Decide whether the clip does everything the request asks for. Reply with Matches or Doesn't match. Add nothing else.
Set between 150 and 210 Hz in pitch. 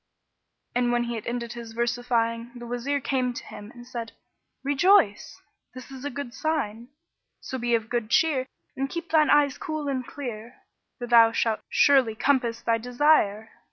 Doesn't match